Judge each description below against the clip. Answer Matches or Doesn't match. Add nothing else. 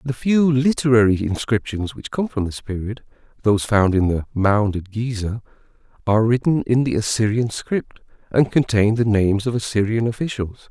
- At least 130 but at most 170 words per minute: Matches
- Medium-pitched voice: Doesn't match